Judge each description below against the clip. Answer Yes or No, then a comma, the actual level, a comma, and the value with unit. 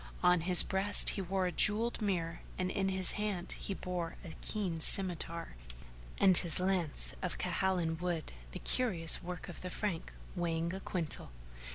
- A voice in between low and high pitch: Yes, medium, 180 Hz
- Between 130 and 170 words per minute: Yes, average, 165 wpm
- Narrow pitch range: Yes, narrow, 2.3 semitones